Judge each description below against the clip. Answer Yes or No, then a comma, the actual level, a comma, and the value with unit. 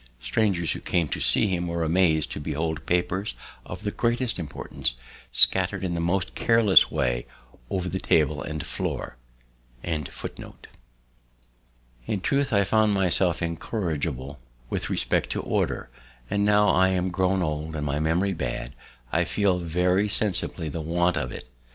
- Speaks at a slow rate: No, average, 150 wpm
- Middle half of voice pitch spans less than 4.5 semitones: Yes, average, 3.8 semitones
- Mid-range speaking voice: No, very low, 90 Hz